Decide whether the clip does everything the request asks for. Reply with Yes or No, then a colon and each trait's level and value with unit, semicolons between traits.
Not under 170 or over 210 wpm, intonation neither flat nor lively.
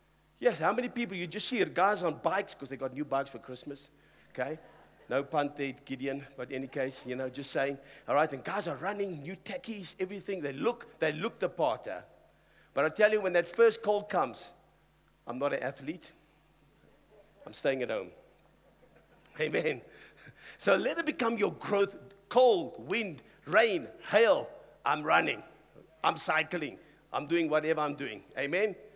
No: average, 175 wpm; wide, 7.1 semitones